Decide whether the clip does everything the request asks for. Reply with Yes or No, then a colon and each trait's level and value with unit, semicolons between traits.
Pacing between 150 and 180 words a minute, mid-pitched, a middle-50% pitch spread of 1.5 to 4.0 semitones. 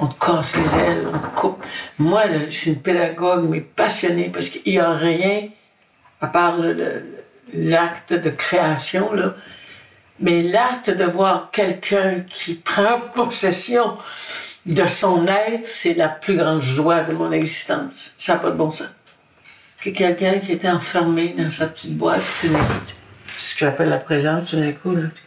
Yes: average, 170 wpm; medium, 175 Hz; average, 3.4 semitones